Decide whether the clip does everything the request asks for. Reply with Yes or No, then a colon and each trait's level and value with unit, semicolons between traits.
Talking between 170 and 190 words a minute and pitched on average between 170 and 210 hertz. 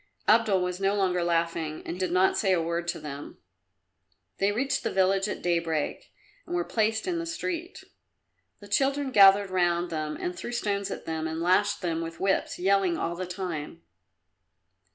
Yes: average, 175 wpm; medium, 185 Hz